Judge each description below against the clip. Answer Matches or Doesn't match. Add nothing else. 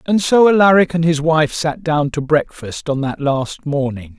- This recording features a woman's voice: Doesn't match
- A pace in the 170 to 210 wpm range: Matches